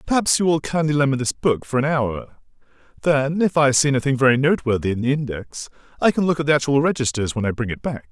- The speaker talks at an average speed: No, fast, 235 wpm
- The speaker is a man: Yes, male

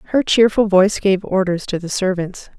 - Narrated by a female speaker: Yes, female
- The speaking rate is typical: Yes, average, 185 wpm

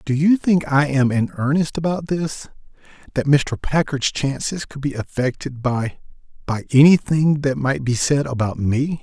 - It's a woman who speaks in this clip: No, male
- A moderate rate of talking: Yes, average, 155 wpm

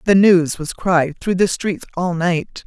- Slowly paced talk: No, fast, 205 wpm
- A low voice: No, medium, 175 Hz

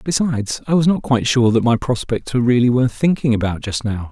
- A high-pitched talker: No, low, 125 Hz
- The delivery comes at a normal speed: No, fast, 235 wpm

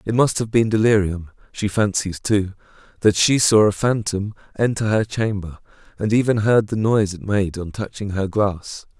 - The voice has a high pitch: No, low, 105 Hz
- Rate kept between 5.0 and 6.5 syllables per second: No, 4.8 syllables/s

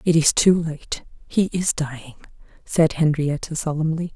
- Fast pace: No, average, 145 wpm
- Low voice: No, medium, 155 Hz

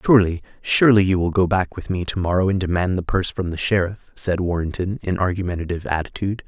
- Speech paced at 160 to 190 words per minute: No, fast, 205 wpm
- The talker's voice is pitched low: Yes, very low, 90 Hz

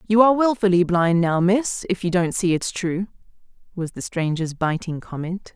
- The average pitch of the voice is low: No, medium, 185 Hz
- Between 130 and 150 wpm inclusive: No, average, 185 wpm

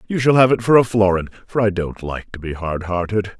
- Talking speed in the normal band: No, fast, 265 wpm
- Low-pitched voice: Yes, low, 100 Hz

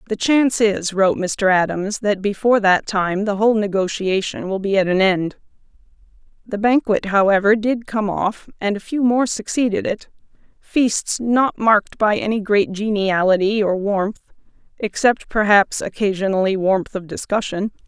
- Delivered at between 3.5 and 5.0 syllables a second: Yes, 4.7 syllables/s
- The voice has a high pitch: Yes, high, 205 Hz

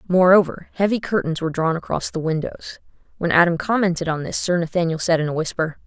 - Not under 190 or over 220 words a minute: Yes, average, 195 wpm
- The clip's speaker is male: No, female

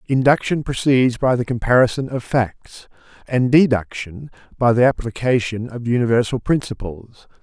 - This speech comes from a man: Yes, male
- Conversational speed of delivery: No, slow, 120 wpm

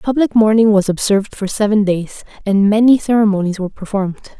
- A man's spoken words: No, female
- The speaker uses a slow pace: No, average, 165 wpm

